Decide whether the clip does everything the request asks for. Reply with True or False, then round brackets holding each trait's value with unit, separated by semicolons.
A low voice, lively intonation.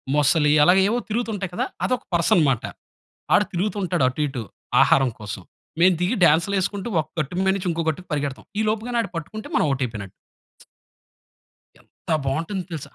False (175 Hz; 5.7 semitones)